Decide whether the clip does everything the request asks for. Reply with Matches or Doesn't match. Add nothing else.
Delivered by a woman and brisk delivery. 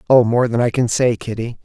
Doesn't match